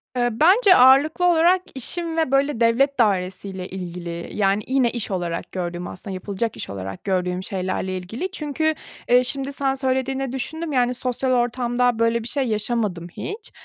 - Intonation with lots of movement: Yes, wide, 6.3 semitones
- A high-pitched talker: Yes, high, 240 Hz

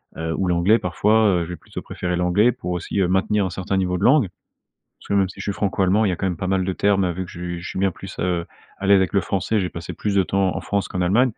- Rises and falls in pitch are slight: Yes, narrow, 2.0 semitones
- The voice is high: No, very low, 95 Hz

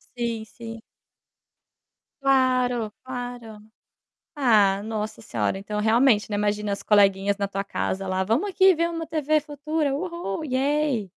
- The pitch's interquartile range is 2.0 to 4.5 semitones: No, wide, 5.5 semitones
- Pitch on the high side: Yes, high, 235 Hz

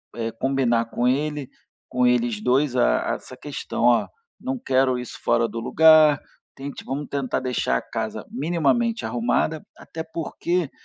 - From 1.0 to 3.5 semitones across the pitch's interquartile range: No, average, 4.2 semitones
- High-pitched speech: No, low, 130 Hz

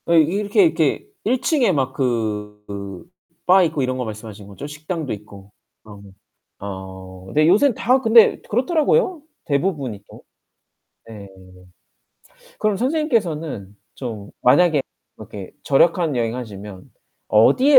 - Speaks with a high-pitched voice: No, low, 135 Hz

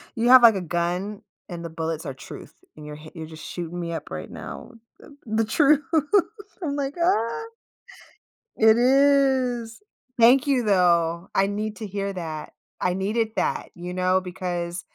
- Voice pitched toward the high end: Yes, high, 195 Hz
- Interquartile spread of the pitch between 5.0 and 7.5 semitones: Yes, wide, 5.5 semitones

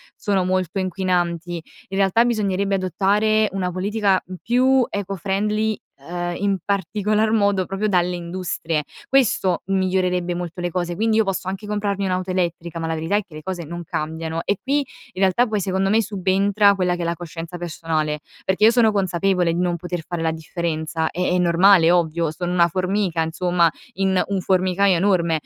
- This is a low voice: No, medium, 185 Hz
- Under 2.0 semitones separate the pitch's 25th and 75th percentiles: No, average, 2.7 semitones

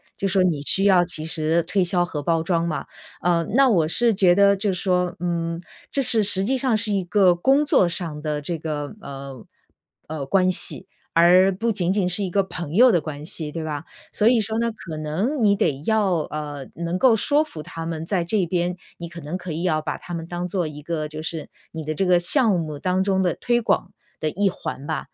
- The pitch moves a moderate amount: Yes, average, 3.8 semitones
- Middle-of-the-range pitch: Yes, medium, 175 Hz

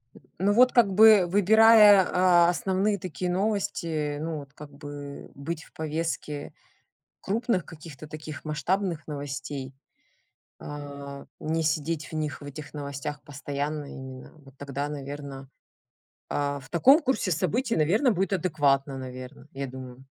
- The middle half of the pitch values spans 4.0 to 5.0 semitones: Yes, average, 4.5 semitones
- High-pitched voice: No, medium, 150 Hz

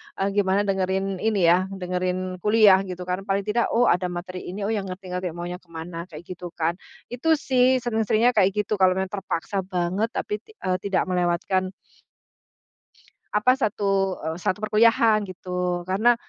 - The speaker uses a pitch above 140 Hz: Yes, high, 190 Hz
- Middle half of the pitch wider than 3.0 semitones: No, narrow, 2.6 semitones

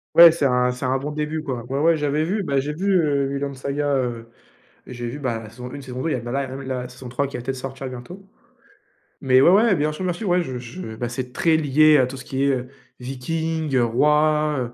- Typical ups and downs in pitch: Yes, average, 3.5 semitones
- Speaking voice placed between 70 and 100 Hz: No, low, 135 Hz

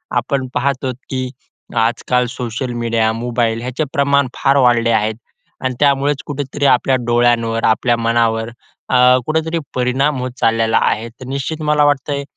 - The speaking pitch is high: No, low, 125 Hz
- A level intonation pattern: No, average, 3.2 semitones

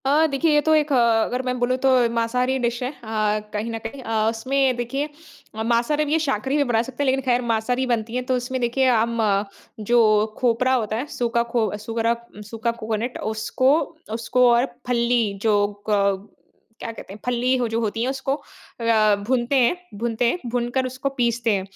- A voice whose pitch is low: No, high, 240 Hz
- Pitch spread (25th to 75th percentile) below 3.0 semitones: Yes, narrow, 2.5 semitones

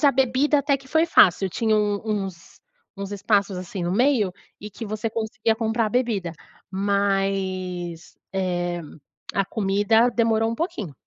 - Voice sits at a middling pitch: No, high, 205 Hz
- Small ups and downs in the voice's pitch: No, average, 3.1 semitones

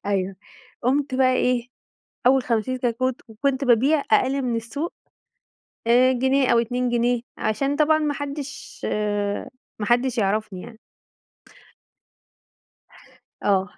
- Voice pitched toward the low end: No, very high, 250 Hz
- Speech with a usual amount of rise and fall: Yes, average, 3.4 semitones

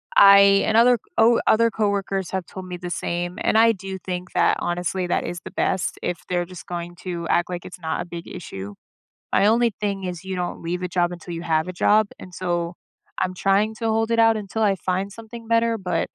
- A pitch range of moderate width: Yes, average, 3.4 semitones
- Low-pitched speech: No, medium, 185 Hz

